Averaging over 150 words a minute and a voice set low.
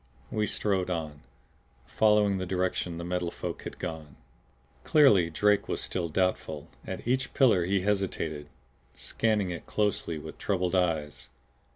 No: average, 140 wpm; very low, 90 Hz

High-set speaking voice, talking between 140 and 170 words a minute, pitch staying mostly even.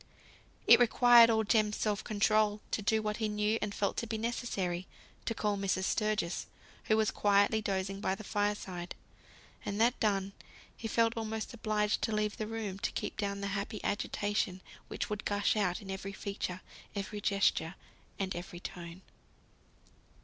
Yes: high, 210 Hz; average, 165 wpm; narrow, 1.8 semitones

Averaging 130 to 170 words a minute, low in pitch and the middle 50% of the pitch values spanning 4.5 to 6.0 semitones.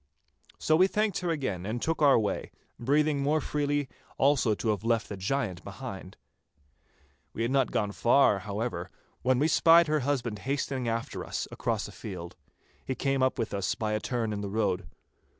No: average, 185 wpm; low, 125 Hz; average, 5.3 semitones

